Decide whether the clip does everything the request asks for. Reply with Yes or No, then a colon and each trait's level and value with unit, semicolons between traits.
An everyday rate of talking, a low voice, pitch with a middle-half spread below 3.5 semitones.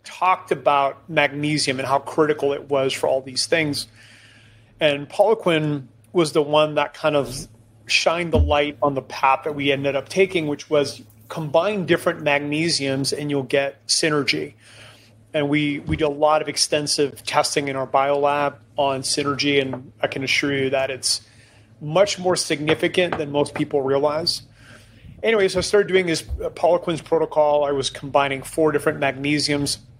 No: average, 170 wpm; medium, 145 Hz; average, 2.7 semitones